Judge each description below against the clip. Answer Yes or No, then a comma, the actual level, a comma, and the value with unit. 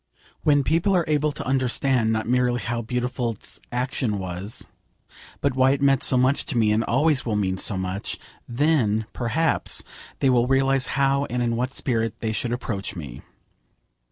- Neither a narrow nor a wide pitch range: Yes, average, 3.5 semitones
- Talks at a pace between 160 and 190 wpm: Yes, average, 175 wpm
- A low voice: Yes, low, 125 Hz